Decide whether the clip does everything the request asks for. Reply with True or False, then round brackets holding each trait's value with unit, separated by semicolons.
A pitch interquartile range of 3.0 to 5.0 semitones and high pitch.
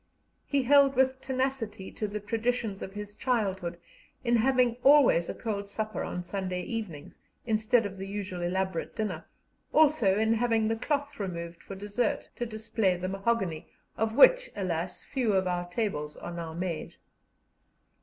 True (4.4 semitones; 210 Hz)